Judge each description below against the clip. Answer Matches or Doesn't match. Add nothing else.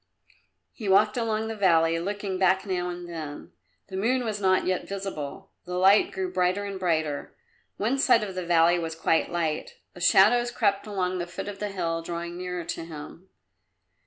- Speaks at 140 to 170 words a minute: Doesn't match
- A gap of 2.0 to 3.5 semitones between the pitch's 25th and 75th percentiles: Matches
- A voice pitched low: Doesn't match